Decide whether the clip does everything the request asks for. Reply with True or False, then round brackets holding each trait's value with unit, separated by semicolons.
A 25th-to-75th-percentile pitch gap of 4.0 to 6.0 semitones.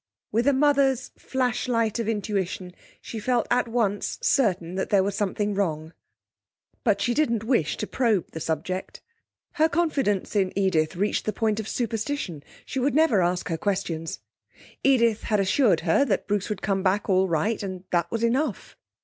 True (4.4 semitones)